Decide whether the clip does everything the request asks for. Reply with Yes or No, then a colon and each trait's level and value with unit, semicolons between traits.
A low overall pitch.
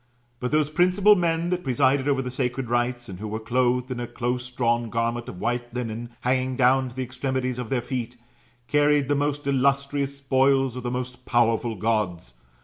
Yes: low, 125 Hz